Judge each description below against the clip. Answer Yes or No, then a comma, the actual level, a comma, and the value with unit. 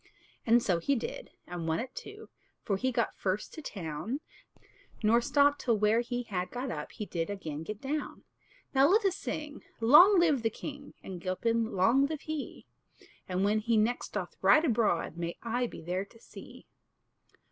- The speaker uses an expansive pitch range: Yes, wide, 6.4 semitones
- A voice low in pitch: No, high, 230 Hz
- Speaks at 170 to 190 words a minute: Yes, average, 180 wpm